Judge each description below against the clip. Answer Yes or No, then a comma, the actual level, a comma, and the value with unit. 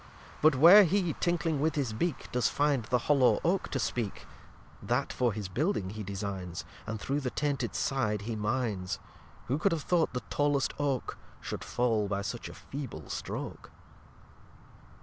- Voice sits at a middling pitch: No, low, 130 Hz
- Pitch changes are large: Yes, wide, 5.7 semitones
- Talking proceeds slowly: No, average, 165 wpm